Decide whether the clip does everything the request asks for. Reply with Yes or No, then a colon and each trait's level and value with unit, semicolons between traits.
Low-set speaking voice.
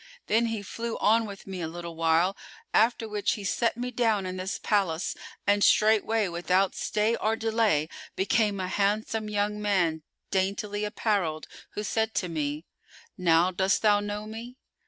No: high, 205 Hz